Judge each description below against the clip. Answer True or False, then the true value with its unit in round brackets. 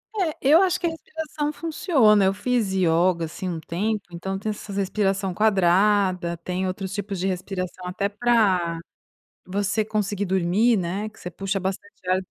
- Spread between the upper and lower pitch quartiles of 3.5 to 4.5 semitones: False (2.8 semitones)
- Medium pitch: False (195 Hz)